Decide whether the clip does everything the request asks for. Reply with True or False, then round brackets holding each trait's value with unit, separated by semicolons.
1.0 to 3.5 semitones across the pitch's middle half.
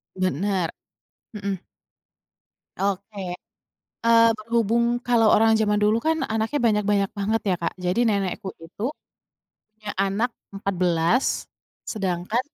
True (2.8 semitones)